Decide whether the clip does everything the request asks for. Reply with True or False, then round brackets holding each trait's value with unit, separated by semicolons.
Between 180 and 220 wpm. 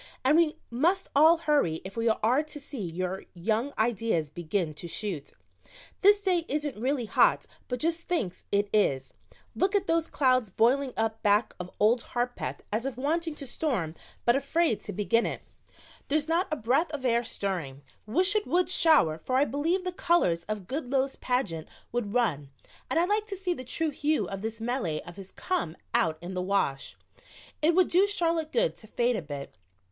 True (190 wpm)